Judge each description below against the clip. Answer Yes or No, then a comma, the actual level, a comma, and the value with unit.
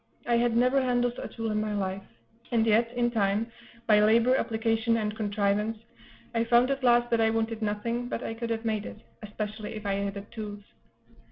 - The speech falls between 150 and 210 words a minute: Yes, average, 200 wpm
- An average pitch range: No, narrow, 2.0 semitones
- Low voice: No, high, 225 Hz